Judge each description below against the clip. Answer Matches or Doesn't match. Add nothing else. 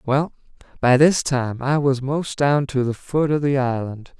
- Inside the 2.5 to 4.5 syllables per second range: Matches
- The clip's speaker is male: Matches